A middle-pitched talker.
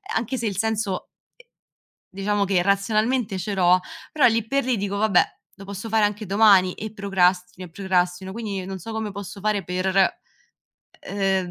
No: high, 200 Hz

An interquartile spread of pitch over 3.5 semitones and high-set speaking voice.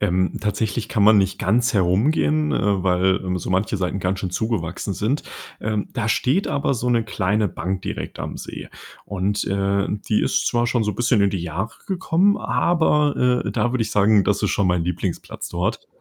No: average, 4.1 semitones; low, 105 Hz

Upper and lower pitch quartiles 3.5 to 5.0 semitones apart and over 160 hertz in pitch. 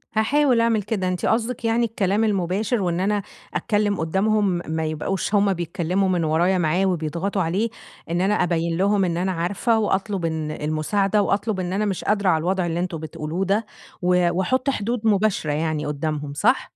Yes: average, 3.8 semitones; high, 190 Hz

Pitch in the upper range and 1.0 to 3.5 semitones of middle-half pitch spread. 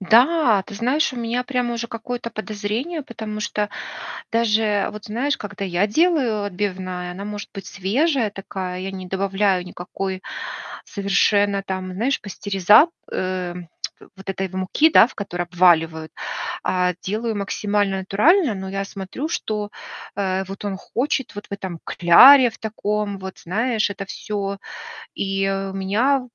Yes: high, 205 Hz; average, 3.2 semitones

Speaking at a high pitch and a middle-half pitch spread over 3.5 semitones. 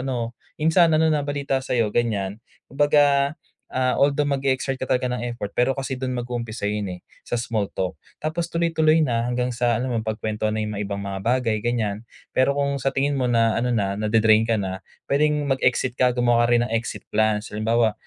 No: low, 120 Hz; average, 4.0 semitones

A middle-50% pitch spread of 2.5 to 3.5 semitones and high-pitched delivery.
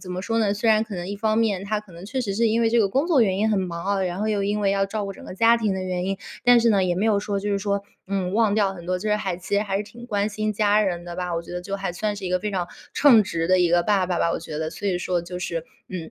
Yes: average, 2.8 semitones; high, 200 Hz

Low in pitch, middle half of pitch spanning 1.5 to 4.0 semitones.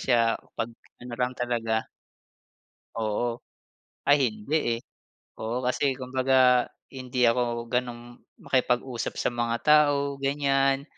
Yes: low, 125 Hz; narrow, 2.4 semitones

